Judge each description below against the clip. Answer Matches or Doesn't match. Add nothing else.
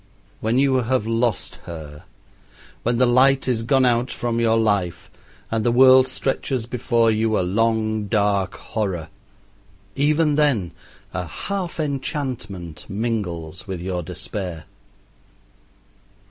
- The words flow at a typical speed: Doesn't match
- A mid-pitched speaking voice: Doesn't match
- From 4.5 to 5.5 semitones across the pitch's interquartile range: Matches